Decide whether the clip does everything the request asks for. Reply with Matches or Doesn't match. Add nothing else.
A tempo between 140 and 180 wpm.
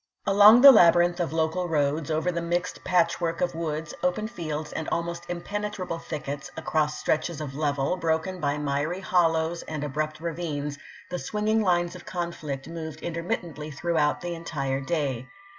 Matches